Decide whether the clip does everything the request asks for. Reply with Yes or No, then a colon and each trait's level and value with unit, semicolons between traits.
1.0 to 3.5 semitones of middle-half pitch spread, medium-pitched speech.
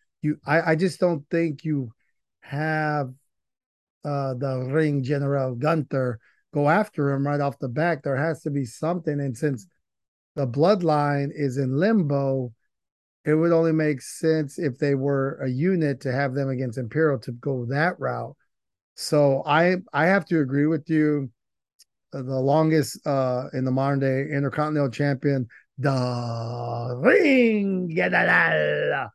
Yes: average, 3.0 semitones; medium, 145 Hz